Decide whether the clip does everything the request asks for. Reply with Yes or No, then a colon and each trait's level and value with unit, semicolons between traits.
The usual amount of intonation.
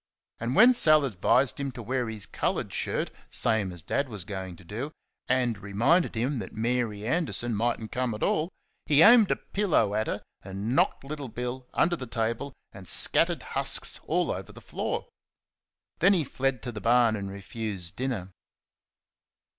Yes: average, 4.8 semitones